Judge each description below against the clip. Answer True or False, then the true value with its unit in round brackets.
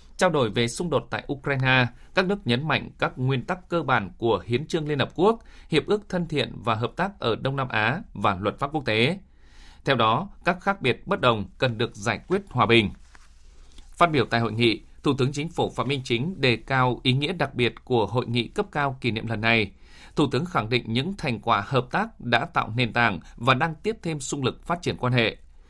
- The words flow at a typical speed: True (235 wpm)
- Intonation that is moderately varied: True (4.7 semitones)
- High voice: False (125 Hz)